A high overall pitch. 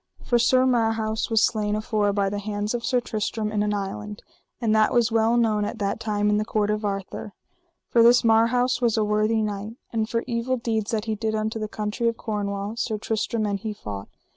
Yes: high, 215 Hz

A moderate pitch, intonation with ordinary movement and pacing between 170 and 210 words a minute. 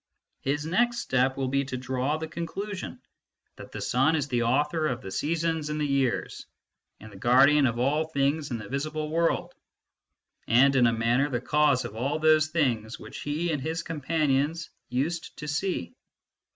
Yes: medium, 145 Hz; average, 3.6 semitones; average, 180 wpm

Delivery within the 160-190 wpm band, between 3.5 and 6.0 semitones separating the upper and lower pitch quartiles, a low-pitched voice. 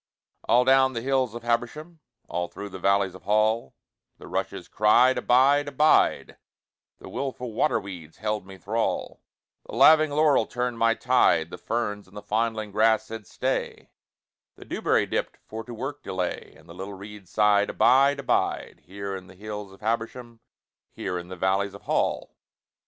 Yes: average, 165 wpm; average, 4.2 semitones; low, 110 Hz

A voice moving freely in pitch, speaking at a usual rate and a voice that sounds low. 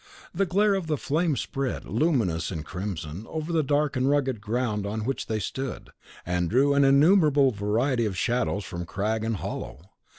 Yes: wide, 6.0 semitones; average, 175 wpm; low, 125 Hz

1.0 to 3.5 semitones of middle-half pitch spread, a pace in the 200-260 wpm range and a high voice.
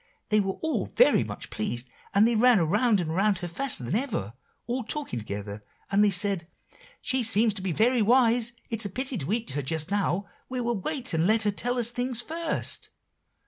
No: average, 5.3 semitones; fast, 205 wpm; high, 215 Hz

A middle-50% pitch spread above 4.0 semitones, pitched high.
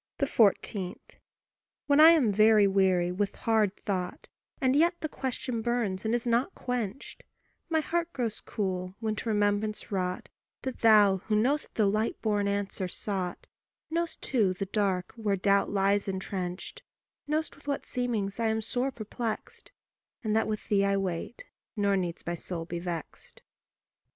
No: average, 3.7 semitones; high, 210 Hz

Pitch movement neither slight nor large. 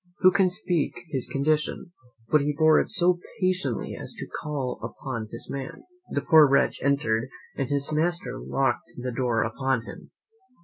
Yes: average, 3.6 semitones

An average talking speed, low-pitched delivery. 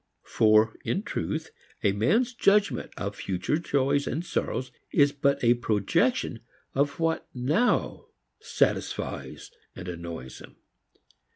No: slow, 115 wpm; low, 130 Hz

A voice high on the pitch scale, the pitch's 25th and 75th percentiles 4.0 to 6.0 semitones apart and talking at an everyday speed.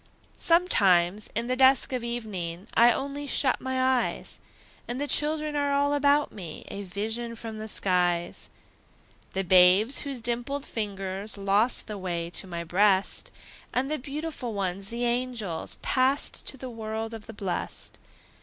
Yes: high, 225 Hz; average, 5.3 semitones; average, 155 wpm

